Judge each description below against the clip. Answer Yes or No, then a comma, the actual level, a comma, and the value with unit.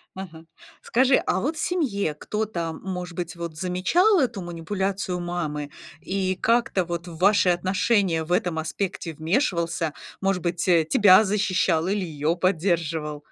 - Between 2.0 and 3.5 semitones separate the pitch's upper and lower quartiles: Yes, average, 3.2 semitones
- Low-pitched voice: No, medium, 180 Hz